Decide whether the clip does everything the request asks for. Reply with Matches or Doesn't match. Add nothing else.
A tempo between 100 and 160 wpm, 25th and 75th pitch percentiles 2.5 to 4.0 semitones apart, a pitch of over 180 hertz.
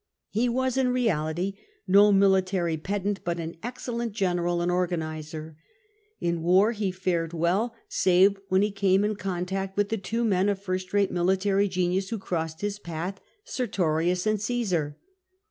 Matches